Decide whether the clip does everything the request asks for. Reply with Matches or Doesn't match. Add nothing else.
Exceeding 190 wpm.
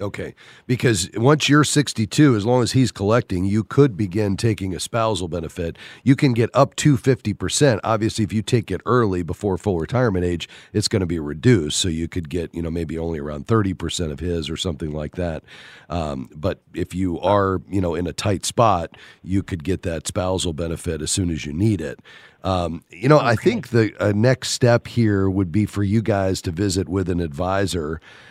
Matches